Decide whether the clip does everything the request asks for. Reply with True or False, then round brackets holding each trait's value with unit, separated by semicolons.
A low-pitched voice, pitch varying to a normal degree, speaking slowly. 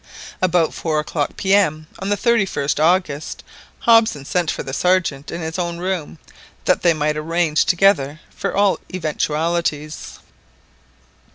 False (170 Hz; 3.4 semitones; 130 wpm)